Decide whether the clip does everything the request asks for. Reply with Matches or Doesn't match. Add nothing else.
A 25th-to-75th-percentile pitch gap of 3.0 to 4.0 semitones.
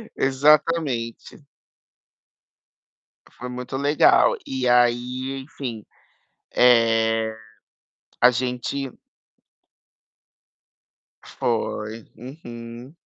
Doesn't match